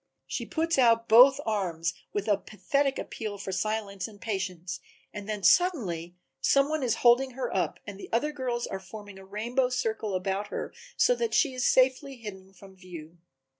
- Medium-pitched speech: No, high, 215 Hz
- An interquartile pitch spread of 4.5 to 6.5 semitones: Yes, average, 5.0 semitones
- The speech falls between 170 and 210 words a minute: Yes, average, 180 wpm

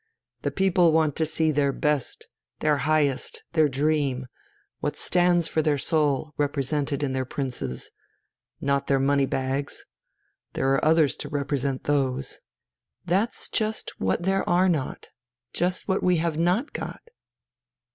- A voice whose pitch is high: No, medium, 150 Hz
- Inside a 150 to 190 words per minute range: No, average, 140 wpm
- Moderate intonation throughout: Yes, average, 3.5 semitones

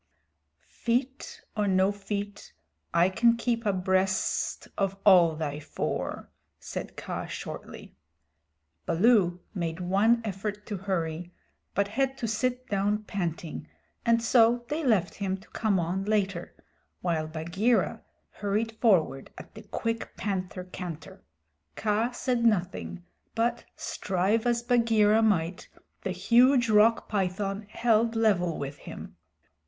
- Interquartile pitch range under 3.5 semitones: No, average, 4.0 semitones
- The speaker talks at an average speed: No, slow, 125 wpm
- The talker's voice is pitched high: Yes, high, 205 Hz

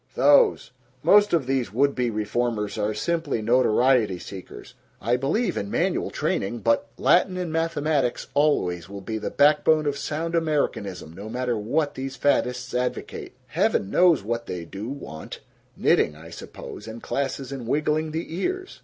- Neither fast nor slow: Yes, average, 155 wpm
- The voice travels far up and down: Yes, wide, 6.2 semitones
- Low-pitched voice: Yes, low, 125 Hz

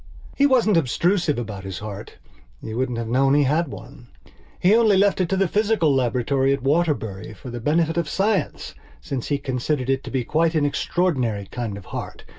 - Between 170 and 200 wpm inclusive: Yes, average, 195 wpm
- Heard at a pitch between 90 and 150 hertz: Yes, medium, 140 Hz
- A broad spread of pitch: Yes, wide, 6.0 semitones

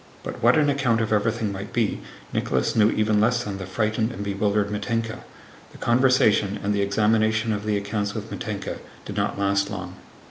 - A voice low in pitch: Yes, low, 105 Hz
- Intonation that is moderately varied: No, narrow, 1.9 semitones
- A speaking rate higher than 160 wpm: Yes, average, 185 wpm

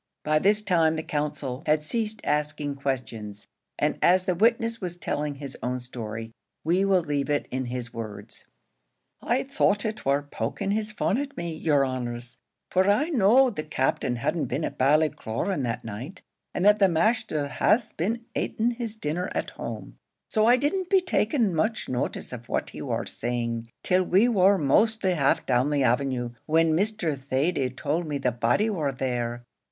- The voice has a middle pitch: Yes, medium, 155 Hz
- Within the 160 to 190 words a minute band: Yes, average, 175 wpm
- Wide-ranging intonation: Yes, wide, 8.1 semitones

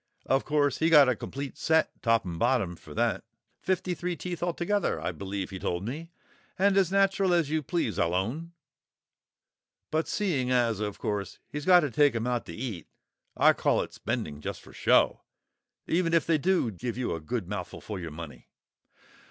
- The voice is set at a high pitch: No, low, 130 Hz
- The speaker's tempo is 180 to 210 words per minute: Yes, average, 190 wpm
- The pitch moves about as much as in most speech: No, wide, 8.7 semitones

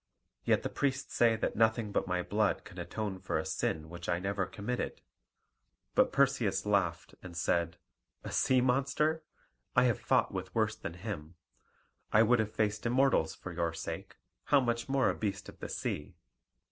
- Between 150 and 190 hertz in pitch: No, low, 105 Hz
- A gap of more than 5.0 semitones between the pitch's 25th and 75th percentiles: Yes, wide, 5.5 semitones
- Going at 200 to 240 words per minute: No, average, 175 wpm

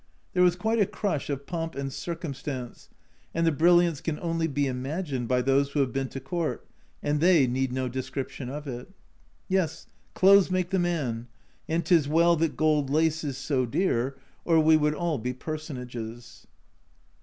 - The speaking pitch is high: No, medium, 150 Hz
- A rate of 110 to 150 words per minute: No, average, 175 wpm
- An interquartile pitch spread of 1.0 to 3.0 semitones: No, average, 4.2 semitones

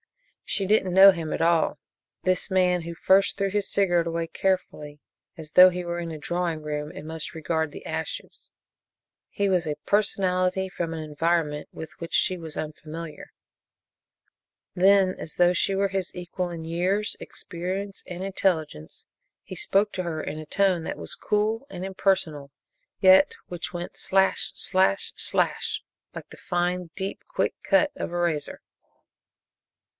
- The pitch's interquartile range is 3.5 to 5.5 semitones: No, average, 2.9 semitones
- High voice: No, medium, 175 Hz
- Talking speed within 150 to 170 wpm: Yes, average, 160 wpm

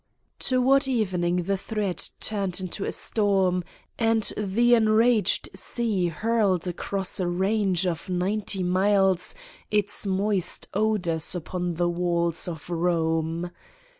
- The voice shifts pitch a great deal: No, average, 3.3 semitones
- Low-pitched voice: No, high, 190 Hz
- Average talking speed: No, slow, 115 wpm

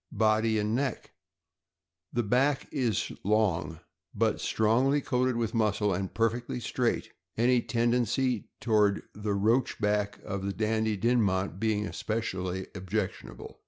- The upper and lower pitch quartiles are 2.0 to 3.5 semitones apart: Yes, average, 2.9 semitones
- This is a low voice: Yes, low, 110 Hz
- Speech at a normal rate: No, slow, 125 wpm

